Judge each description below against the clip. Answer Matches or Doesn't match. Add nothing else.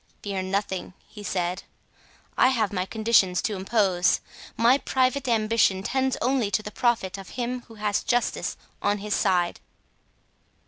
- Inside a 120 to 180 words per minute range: Matches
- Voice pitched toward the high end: Matches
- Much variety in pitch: Doesn't match